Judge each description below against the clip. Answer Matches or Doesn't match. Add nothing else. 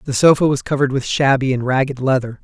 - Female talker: Doesn't match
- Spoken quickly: Matches